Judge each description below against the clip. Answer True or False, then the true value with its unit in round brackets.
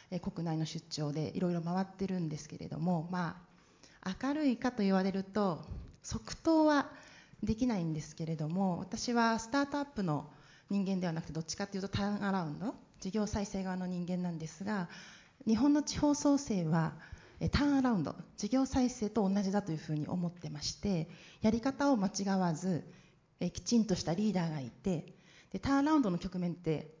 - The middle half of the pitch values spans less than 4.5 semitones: False (5.1 semitones)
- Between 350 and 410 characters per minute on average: True (365 characters per minute)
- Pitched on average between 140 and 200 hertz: True (190 Hz)